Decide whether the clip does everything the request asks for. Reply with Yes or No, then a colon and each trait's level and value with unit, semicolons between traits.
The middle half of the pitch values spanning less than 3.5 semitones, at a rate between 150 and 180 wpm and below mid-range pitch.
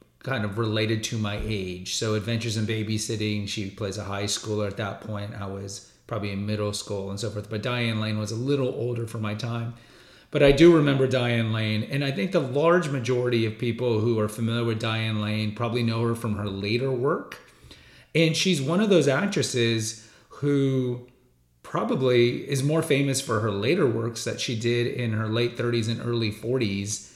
No: average, 2.9 semitones; average, 195 wpm; low, 115 Hz